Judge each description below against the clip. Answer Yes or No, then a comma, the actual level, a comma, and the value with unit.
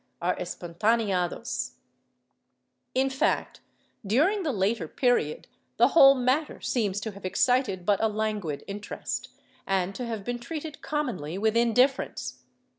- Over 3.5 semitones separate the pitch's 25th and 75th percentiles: Yes, average, 4.9 semitones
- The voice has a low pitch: No, high, 220 Hz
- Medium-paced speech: No, slow, 125 wpm